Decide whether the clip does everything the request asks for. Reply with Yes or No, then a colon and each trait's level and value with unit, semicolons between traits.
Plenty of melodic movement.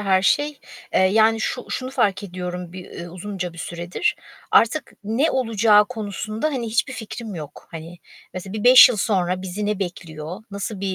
No: average, 3.8 semitones